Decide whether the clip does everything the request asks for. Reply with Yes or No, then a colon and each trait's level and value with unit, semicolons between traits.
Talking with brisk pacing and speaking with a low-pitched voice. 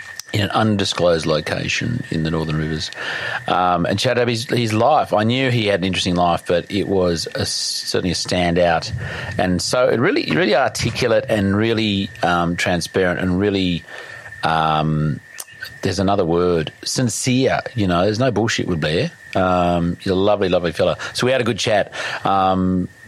No: average, 165 wpm; very low, 95 Hz